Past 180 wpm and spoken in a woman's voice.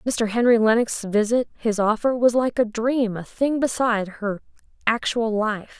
No: average, 145 wpm; female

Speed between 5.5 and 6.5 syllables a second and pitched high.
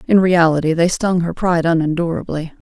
No: 5.8 syllables/s; medium, 170 Hz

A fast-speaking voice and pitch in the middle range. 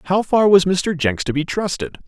Yes: fast, 230 wpm; medium, 180 Hz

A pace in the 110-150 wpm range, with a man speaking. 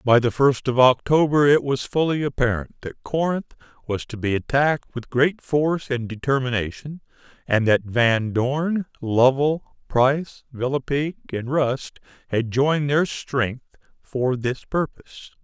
Yes: average, 140 wpm; male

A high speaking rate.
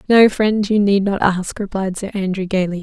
Yes: fast, 215 wpm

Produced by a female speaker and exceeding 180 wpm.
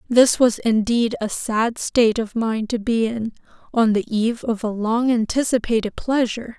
No: female; average, 175 wpm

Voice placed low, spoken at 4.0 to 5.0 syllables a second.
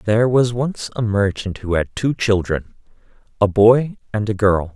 Yes: low, 105 Hz; 4.5 syllables/s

